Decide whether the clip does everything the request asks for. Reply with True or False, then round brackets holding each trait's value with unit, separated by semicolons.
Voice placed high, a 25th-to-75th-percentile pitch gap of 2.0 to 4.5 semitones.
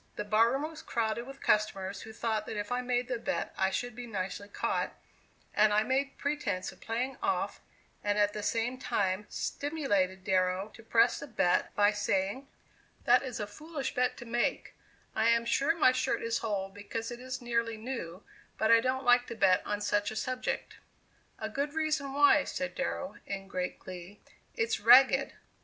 True (230 Hz; 4.0 semitones)